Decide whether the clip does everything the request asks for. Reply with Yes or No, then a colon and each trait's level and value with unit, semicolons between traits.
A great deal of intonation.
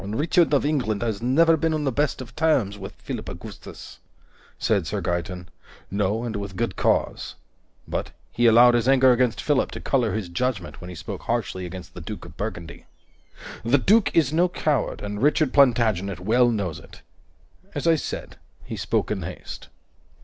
Yes: wide, 5.9 semitones